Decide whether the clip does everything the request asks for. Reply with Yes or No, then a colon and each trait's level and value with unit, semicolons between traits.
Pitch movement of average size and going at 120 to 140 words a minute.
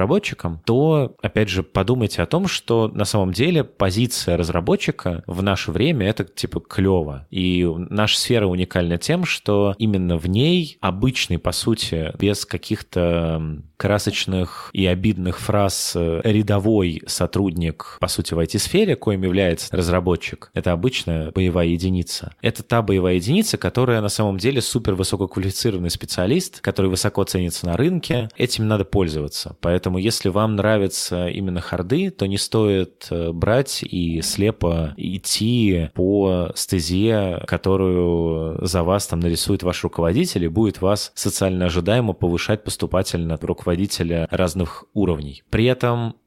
Yes: average, 3.7 semitones; average, 135 wpm